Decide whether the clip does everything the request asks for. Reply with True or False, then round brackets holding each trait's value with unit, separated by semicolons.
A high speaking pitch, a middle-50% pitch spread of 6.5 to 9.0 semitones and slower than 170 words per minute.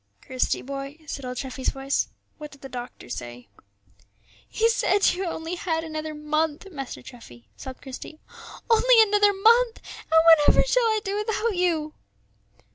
True (315 Hz; 7.2 semitones; 150 wpm)